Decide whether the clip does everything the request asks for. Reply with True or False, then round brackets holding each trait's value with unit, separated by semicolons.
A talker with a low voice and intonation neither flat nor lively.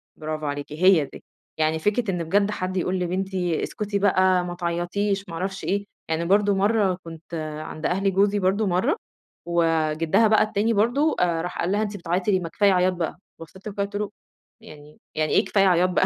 False (185 Hz; 3.1 semitones)